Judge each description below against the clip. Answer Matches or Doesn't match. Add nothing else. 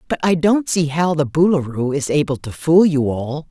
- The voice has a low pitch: Doesn't match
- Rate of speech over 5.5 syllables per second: Doesn't match